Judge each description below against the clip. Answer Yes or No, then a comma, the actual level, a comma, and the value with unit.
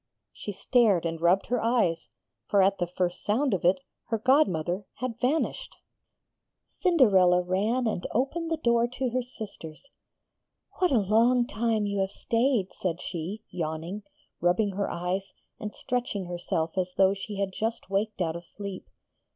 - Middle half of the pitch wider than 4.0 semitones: Yes, average, 4.8 semitones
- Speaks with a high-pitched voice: Yes, high, 200 Hz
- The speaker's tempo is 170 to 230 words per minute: No, average, 160 wpm